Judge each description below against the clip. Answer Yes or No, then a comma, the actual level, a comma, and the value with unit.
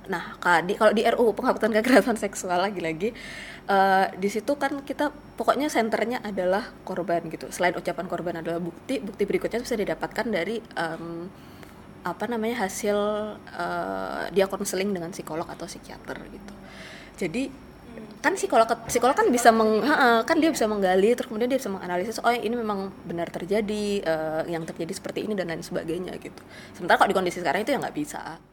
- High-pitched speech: Yes, high, 205 Hz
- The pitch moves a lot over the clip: No, average, 4.7 semitones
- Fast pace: Yes, fast, 170 wpm